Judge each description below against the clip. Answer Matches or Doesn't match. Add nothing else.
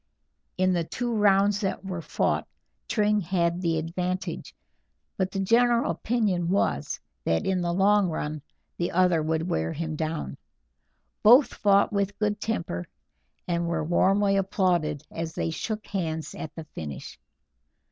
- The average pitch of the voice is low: Doesn't match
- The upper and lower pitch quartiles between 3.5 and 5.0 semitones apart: Matches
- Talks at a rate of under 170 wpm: Matches